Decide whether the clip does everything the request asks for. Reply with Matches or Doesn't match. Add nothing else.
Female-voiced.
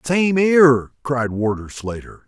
Doesn't match